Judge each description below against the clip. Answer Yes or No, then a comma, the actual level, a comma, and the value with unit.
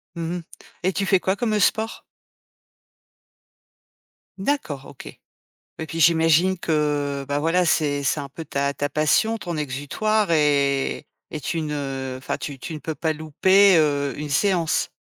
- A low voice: No, medium, 155 Hz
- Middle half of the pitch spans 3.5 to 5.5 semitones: Yes, average, 4.0 semitones